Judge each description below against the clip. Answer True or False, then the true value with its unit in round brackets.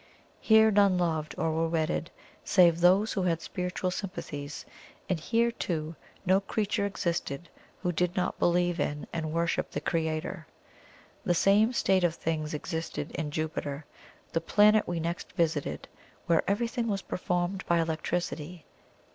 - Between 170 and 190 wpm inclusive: False (145 wpm)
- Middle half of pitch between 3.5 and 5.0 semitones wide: False (3.0 semitones)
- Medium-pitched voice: True (175 Hz)